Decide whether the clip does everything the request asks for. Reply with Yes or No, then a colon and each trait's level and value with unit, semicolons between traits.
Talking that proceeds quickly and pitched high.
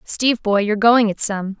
Yes: fast, 225 wpm; high, 215 Hz